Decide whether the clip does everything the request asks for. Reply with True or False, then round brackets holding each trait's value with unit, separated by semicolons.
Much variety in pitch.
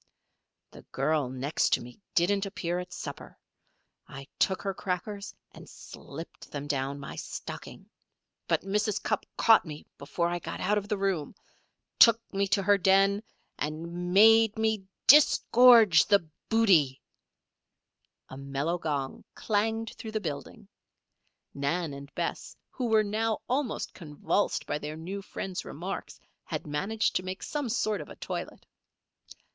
True (5.9 semitones)